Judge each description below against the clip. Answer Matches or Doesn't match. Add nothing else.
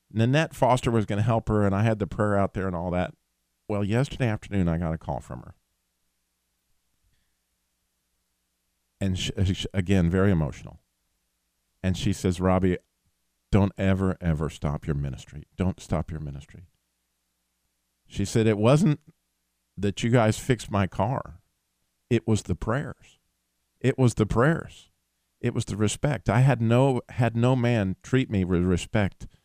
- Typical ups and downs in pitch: Doesn't match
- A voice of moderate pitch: Doesn't match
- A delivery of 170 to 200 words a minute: Doesn't match